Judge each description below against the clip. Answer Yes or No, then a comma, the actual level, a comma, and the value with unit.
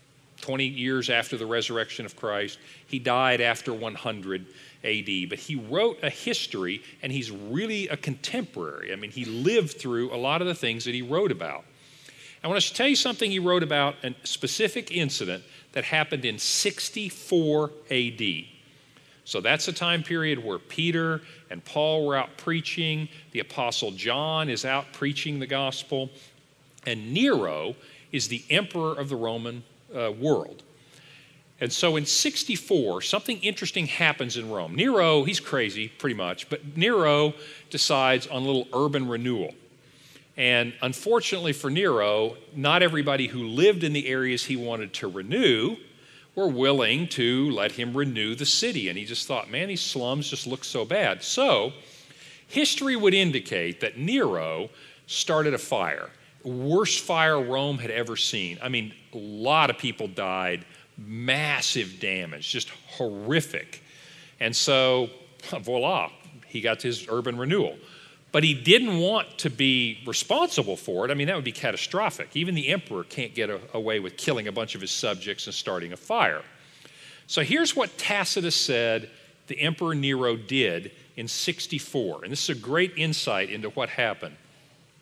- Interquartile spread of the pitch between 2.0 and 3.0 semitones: No, average, 4.5 semitones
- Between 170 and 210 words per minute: No, average, 160 wpm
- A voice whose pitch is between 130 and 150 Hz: Yes, medium, 140 Hz